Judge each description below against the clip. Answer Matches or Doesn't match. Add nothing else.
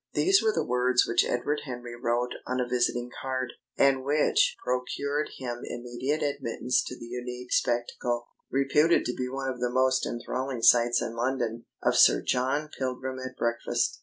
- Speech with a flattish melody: Matches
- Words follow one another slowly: Doesn't match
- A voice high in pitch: Doesn't match